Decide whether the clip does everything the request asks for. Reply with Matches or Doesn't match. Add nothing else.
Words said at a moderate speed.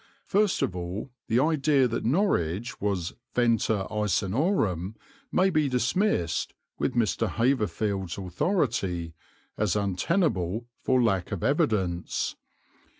Doesn't match